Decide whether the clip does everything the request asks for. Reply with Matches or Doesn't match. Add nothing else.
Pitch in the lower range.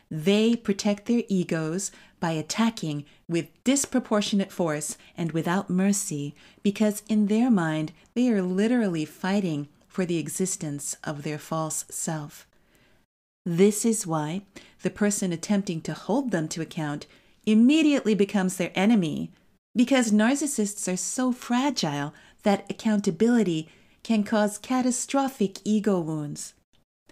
Doesn't match